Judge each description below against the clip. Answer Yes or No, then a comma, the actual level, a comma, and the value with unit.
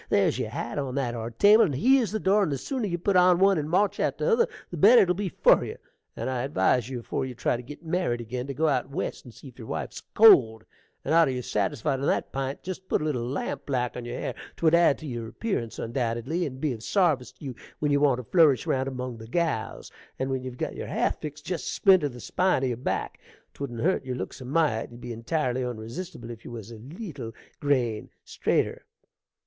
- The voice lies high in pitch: No, low, 135 Hz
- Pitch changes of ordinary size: No, wide, 5.9 semitones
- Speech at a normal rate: No, fast, 240 wpm